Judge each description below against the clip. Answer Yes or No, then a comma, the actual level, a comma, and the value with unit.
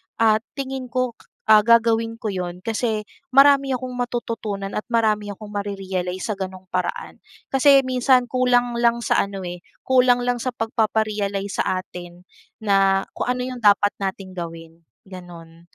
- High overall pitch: Yes, high, 215 Hz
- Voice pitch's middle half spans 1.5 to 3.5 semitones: No, average, 4.4 semitones